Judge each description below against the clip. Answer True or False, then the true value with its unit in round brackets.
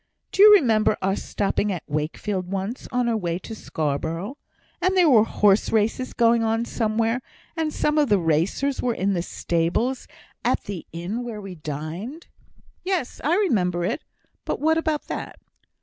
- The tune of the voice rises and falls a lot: True (6.3 semitones)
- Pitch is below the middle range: False (215 Hz)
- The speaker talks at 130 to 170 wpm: True (165 wpm)